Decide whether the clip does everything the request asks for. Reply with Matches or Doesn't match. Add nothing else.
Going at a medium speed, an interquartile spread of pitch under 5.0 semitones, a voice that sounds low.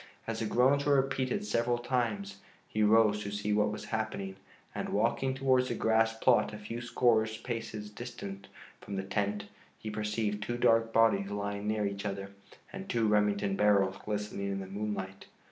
Matches